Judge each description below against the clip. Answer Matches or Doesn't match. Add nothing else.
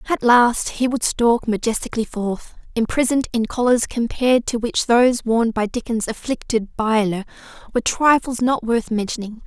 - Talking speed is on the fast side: Doesn't match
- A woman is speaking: Matches